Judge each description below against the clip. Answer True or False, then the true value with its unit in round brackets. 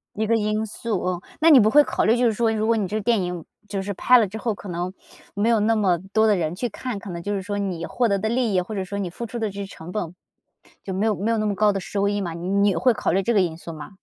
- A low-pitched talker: False (205 Hz)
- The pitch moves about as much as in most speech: True (3.1 semitones)